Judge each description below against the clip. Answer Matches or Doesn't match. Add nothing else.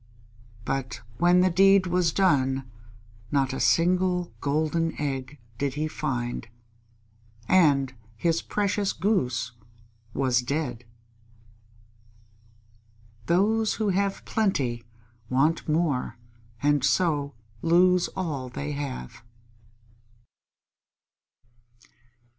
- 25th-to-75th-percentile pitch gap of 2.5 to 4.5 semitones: Doesn't match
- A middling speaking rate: Doesn't match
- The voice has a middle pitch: Matches